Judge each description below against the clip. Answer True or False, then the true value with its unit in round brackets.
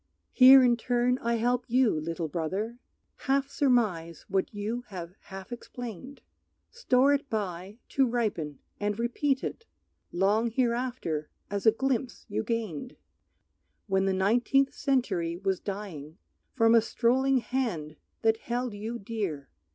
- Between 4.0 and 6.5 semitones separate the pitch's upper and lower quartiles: True (4.6 semitones)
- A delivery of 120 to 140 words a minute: True (135 wpm)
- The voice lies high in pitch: True (225 Hz)